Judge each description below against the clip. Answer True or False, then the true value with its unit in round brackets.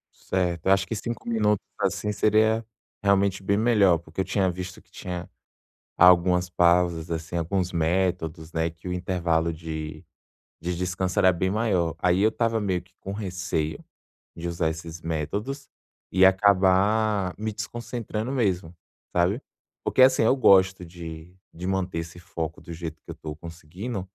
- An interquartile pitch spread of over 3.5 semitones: False (3.2 semitones)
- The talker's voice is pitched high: False (90 Hz)